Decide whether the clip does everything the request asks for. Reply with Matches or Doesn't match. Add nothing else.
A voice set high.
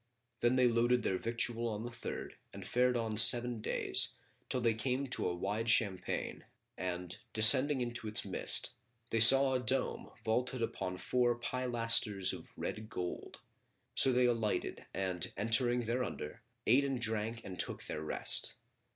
Doesn't match